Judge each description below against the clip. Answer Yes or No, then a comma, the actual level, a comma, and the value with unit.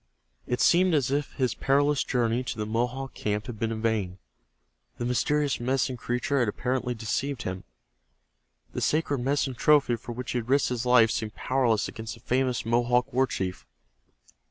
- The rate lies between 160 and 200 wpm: Yes, average, 175 wpm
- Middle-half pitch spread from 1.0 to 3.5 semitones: Yes, average, 2.9 semitones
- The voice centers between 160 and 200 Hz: No, low, 125 Hz